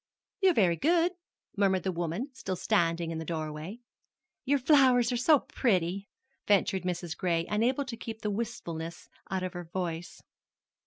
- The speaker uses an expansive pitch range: Yes, wide, 6.3 semitones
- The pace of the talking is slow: No, average, 155 wpm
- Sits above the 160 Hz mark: Yes, high, 190 Hz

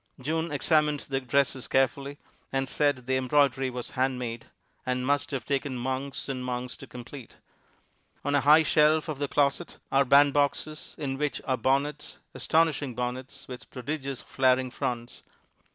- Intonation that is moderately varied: No, narrow, 2.2 semitones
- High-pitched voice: No, low, 135 Hz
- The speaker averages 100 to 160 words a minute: Yes, average, 150 wpm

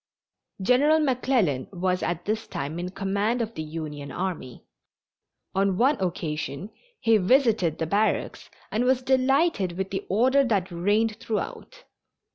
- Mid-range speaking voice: No, high, 200 Hz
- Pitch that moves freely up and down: Yes, wide, 5.9 semitones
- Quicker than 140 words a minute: No, slow, 135 wpm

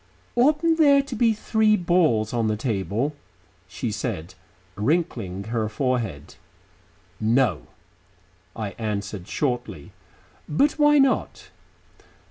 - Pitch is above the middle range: No, low, 120 Hz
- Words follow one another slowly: Yes, slow, 100 wpm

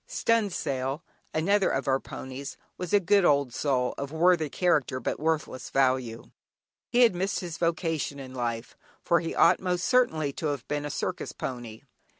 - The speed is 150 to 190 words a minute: Yes, average, 165 wpm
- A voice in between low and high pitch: Yes, medium, 150 Hz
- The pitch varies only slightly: No, average, 5.1 semitones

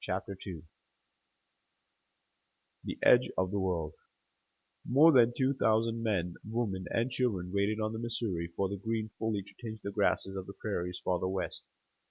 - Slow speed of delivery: No, average, 165 wpm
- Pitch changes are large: No, average, 3.6 semitones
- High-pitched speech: No, low, 105 Hz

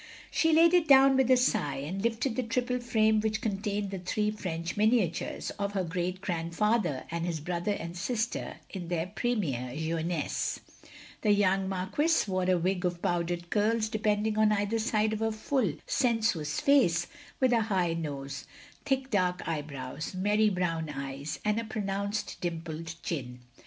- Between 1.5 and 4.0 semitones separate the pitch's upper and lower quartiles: No, average, 4.6 semitones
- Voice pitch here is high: Yes, high, 195 Hz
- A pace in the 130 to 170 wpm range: Yes, average, 160 wpm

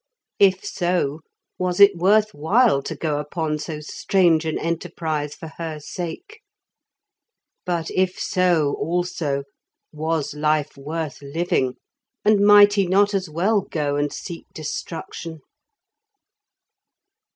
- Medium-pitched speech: Yes, medium, 165 Hz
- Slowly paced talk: Yes, slow, 120 wpm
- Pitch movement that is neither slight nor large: Yes, average, 3.6 semitones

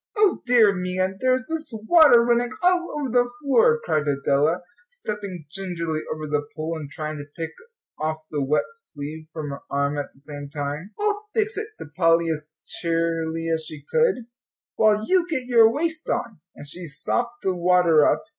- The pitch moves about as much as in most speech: No, wide, 8.5 semitones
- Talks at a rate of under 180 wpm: No, average, 185 wpm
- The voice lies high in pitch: No, medium, 180 Hz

